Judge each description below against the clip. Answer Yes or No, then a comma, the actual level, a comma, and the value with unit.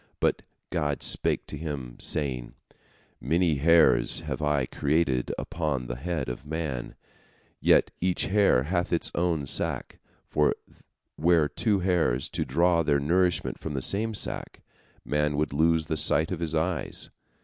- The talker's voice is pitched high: No, very low, 80 Hz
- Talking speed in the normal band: Yes, average, 150 wpm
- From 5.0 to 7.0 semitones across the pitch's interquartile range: No, average, 3.2 semitones